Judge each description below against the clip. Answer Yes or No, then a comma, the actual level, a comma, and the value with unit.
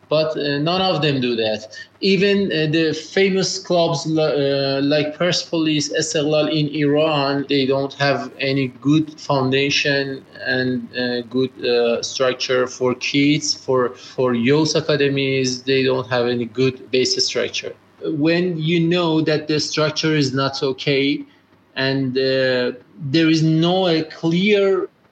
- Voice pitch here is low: No, medium, 145 Hz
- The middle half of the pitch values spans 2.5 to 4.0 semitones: Yes, average, 3.3 semitones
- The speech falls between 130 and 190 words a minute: Yes, average, 140 wpm